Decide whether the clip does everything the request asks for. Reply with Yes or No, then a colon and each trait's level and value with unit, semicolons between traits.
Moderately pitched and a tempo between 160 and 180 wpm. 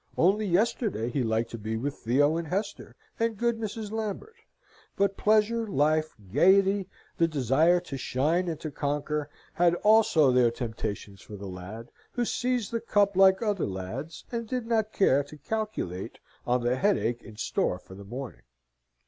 Yes: medium, 160 Hz; average, 165 wpm